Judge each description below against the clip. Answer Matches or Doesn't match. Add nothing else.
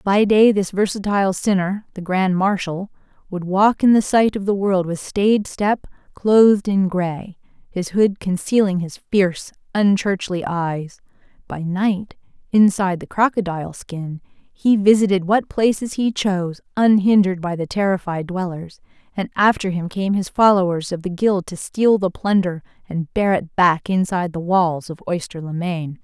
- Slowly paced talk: Doesn't match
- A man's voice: Doesn't match